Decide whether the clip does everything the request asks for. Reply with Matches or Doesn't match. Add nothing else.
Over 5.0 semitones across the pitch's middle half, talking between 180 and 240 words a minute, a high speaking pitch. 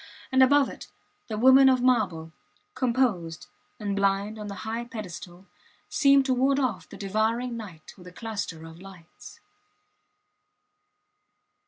Doesn't match